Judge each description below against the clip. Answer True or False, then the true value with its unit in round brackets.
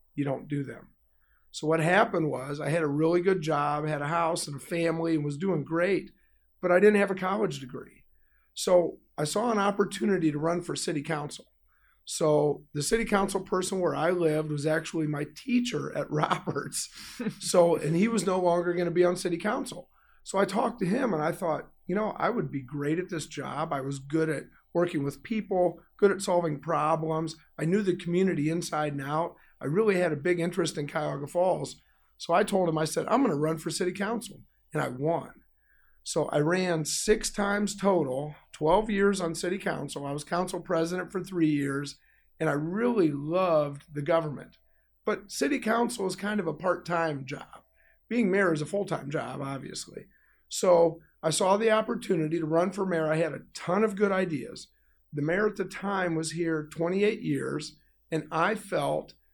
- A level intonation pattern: False (4.1 semitones)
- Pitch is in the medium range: True (170 Hz)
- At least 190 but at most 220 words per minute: True (200 wpm)